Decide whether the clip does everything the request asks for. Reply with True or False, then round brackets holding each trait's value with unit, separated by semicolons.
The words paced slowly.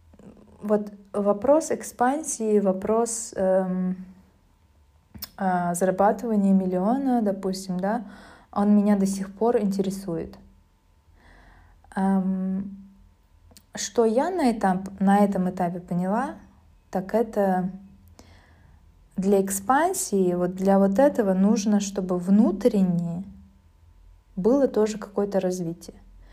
True (90 wpm)